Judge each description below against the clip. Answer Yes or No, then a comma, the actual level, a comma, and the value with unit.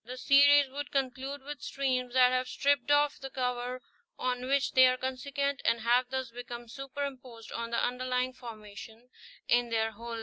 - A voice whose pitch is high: Yes, very high, 255 Hz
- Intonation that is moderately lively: No, narrow, 2.1 semitones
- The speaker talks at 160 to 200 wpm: Yes, average, 175 wpm